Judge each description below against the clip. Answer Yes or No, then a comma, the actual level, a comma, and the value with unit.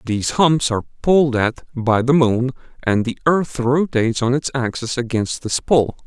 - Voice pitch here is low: Yes, low, 125 Hz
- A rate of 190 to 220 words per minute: No, average, 180 wpm